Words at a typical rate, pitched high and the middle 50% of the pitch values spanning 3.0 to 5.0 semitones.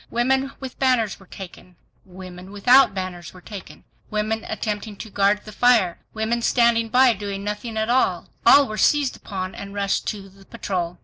Yes: average, 175 wpm; high, 210 Hz; average, 3.5 semitones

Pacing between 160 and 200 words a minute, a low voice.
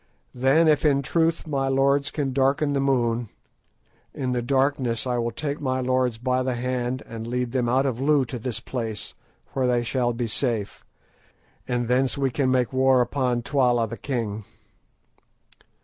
Yes: average, 170 wpm; low, 130 Hz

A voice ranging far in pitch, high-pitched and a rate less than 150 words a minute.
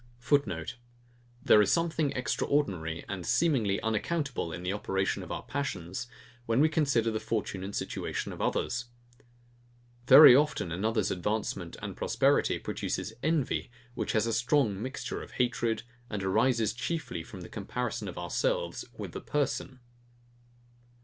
No: wide, 5.8 semitones; low, 115 Hz; average, 140 wpm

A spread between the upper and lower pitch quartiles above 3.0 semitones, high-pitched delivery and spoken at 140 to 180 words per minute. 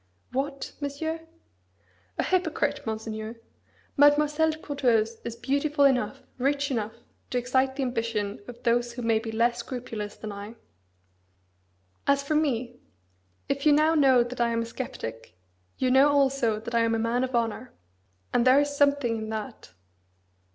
Yes: average, 3.7 semitones; very high, 250 Hz; average, 160 wpm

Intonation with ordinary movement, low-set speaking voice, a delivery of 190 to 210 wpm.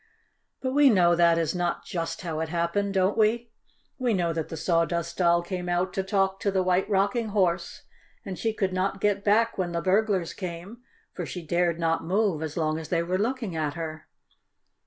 No: average, 3.1 semitones; medium, 185 Hz; average, 200 wpm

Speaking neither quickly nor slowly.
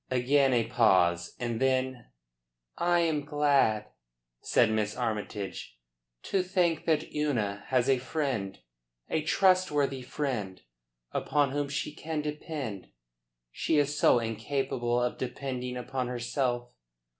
No: slow, 120 wpm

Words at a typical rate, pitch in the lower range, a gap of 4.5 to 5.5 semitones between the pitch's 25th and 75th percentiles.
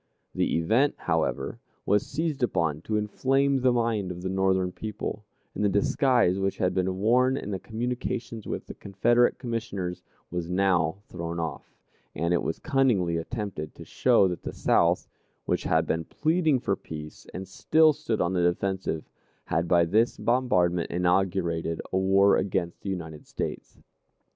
Yes: average, 160 wpm; very low, 95 Hz; average, 5.1 semitones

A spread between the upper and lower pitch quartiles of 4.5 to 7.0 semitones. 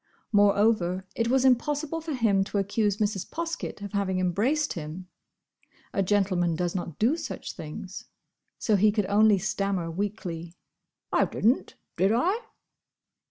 No: average, 3.9 semitones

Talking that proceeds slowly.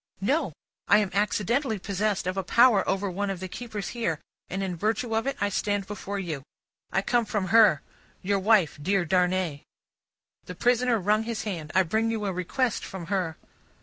No: average, 185 wpm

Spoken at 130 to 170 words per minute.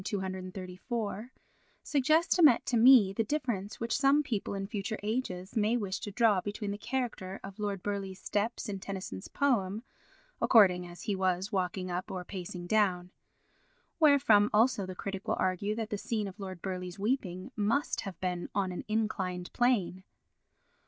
Yes: average, 165 wpm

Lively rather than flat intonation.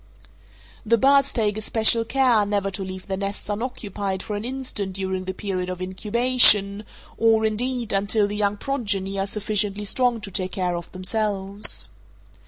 No: average, 2.7 semitones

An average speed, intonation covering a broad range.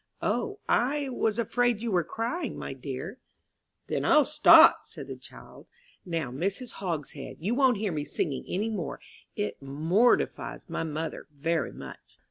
Yes: average, 150 wpm; wide, 7.8 semitones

